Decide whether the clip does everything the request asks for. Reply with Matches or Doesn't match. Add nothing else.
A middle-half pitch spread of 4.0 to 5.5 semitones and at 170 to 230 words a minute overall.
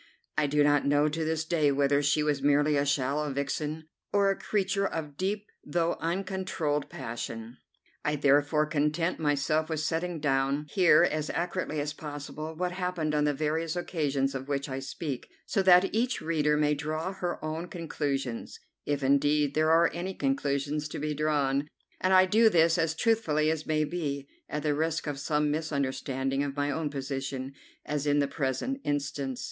Doesn't match